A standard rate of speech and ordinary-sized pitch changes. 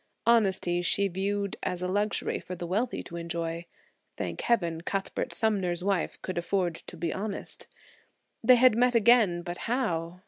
Yes: average, 160 wpm; average, 3.7 semitones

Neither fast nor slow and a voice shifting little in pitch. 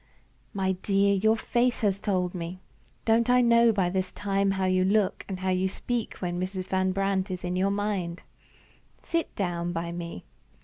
Yes: average, 180 wpm; narrow, 2.0 semitones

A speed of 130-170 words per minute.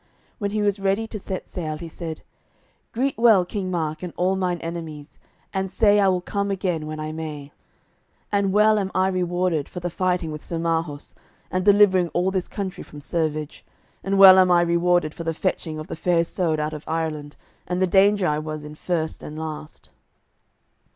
No: average, 195 wpm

